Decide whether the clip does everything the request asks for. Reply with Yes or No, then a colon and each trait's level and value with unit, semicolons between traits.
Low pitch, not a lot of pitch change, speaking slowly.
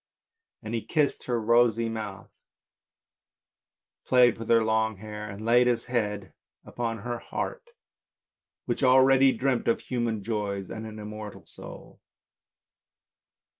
Yes: low, 115 Hz; narrow, 2.2 semitones; slow, 125 wpm